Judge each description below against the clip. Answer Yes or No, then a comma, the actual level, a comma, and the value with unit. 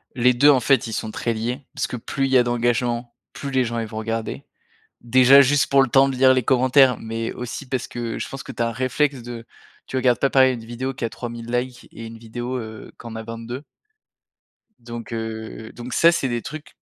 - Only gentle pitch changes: Yes, narrow, 2.2 semitones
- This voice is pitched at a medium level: No, low, 120 Hz